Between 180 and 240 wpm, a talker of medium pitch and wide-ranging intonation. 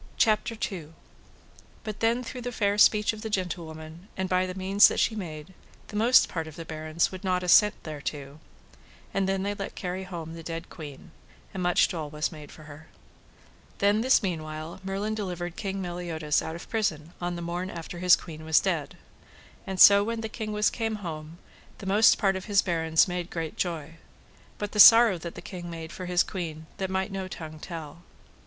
No: average, 195 wpm; medium, 180 Hz; average, 3.7 semitones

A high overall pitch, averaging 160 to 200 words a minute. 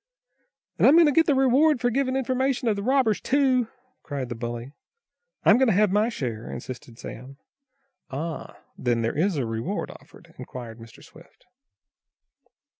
Yes: high, 200 Hz; average, 165 wpm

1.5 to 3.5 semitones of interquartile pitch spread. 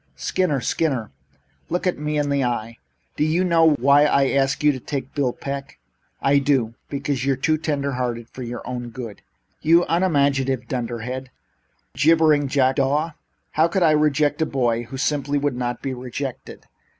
Yes: average, 3.0 semitones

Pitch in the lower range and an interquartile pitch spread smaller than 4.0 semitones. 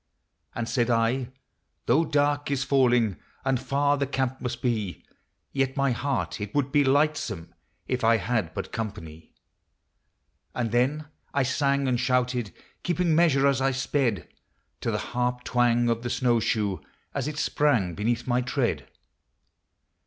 Yes: low, 125 Hz; average, 2.9 semitones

